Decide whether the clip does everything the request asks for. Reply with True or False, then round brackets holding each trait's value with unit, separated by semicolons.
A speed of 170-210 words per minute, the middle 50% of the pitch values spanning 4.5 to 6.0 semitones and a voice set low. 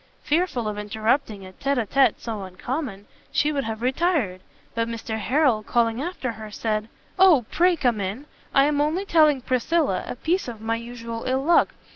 False (180 wpm; 5.1 semitones; 245 Hz)